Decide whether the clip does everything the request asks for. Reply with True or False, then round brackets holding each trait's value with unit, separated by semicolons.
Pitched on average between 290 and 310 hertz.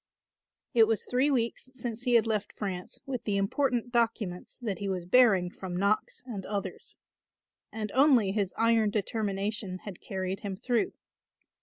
False (215 Hz)